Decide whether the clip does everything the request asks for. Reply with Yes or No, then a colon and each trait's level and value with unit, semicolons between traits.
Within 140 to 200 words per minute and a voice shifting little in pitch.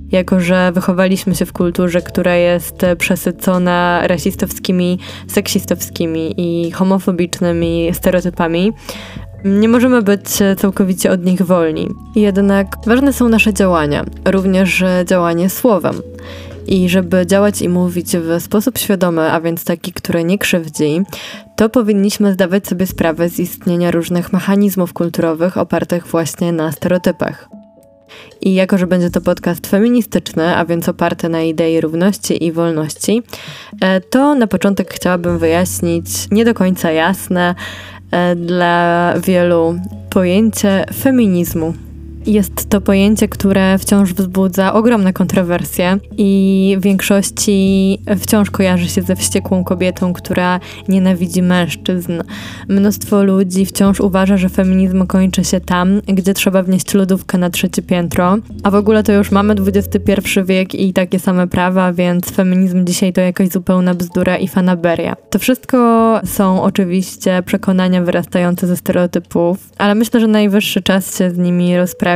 No: average, 130 wpm; narrow, 2.1 semitones